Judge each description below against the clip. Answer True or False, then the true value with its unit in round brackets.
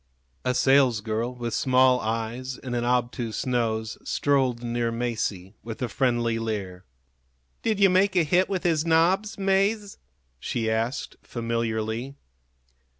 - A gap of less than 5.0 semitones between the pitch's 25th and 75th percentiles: True (4.3 semitones)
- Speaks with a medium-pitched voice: False (120 Hz)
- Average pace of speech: False (130 wpm)